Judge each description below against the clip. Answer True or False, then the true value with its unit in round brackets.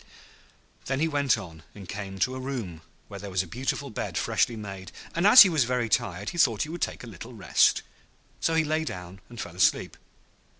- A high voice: False (115 Hz)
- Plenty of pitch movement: True (6.6 semitones)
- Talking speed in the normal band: False (215 wpm)